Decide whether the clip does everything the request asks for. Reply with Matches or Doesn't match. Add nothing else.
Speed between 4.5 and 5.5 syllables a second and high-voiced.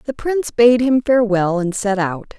Matches